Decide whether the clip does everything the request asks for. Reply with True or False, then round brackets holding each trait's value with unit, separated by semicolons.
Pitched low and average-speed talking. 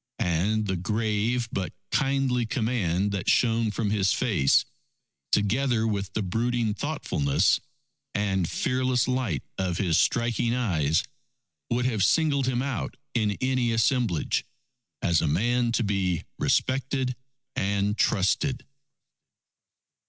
False (110 Hz; 115 wpm)